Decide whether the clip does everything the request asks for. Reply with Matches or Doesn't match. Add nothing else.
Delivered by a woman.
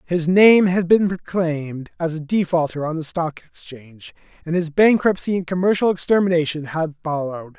Doesn't match